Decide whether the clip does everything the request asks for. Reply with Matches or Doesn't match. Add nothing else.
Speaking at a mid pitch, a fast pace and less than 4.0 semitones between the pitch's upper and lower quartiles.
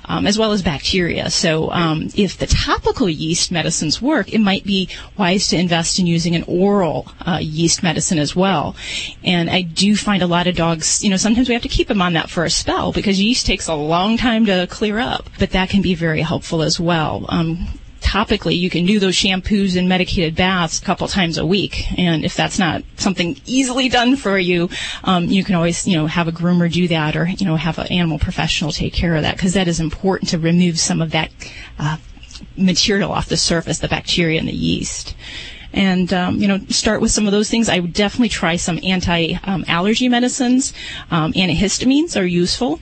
Matches